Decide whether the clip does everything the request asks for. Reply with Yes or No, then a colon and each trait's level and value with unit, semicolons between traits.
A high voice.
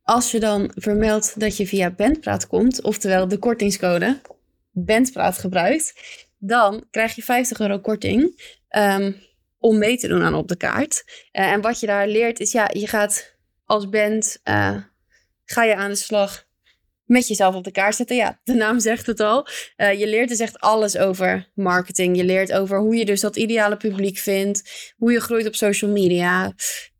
Yes: high, 215 Hz